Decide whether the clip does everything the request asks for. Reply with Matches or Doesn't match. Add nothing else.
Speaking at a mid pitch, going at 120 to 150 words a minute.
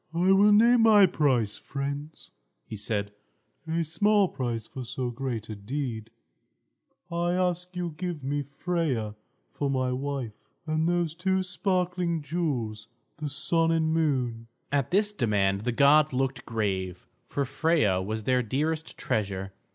Matches